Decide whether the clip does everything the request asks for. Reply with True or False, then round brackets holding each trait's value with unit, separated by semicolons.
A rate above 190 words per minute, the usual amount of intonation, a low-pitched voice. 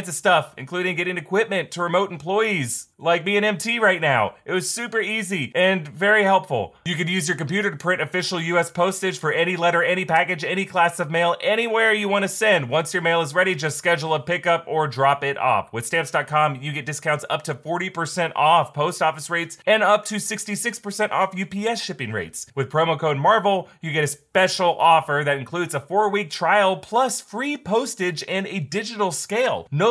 False (200 wpm; 4.0 semitones; 175 Hz)